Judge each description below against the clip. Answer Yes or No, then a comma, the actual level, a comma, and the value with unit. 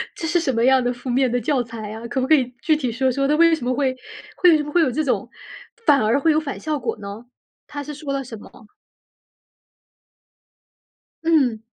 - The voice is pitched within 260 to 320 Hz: Yes, very high, 265 Hz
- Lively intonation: No, average, 3.7 semitones